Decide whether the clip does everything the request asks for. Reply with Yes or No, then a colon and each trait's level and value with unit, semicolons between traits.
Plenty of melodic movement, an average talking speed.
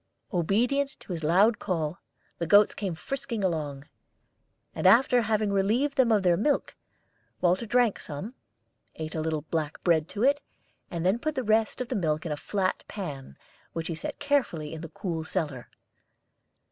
Yes: wide, 6.2 semitones; average, 170 wpm